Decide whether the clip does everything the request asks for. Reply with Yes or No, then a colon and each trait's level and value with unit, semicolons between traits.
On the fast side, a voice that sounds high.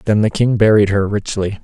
No: fast, 220 wpm; low, 105 Hz